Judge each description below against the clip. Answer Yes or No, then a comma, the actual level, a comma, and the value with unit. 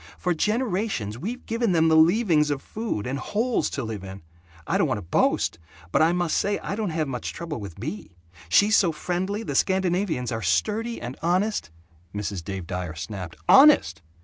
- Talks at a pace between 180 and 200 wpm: Yes, average, 190 wpm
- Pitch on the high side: No, medium, 160 Hz